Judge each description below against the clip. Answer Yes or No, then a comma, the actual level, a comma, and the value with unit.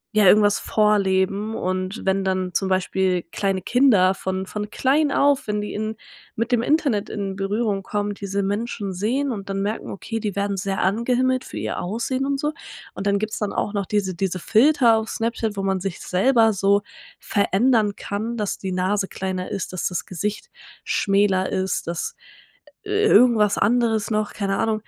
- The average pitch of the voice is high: Yes, high, 205 Hz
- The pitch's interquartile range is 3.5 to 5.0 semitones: No, average, 2.8 semitones